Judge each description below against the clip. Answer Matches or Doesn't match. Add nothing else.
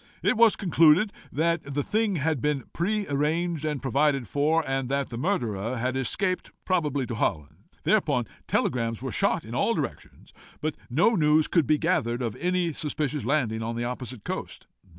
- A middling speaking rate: Matches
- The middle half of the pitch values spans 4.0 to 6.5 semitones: Matches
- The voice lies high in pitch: Doesn't match